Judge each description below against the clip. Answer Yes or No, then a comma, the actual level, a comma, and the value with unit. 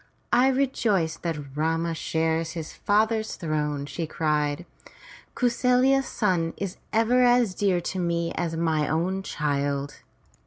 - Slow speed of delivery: Yes, slow, 130 wpm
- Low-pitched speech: No, medium, 170 Hz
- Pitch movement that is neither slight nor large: No, wide, 5.8 semitones